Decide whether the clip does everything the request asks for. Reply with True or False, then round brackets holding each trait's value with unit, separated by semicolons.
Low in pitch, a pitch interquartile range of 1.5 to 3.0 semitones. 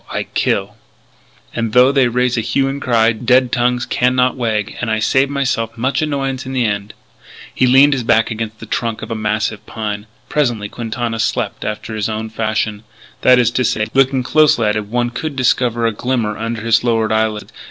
True (115 Hz; 2.6 semitones)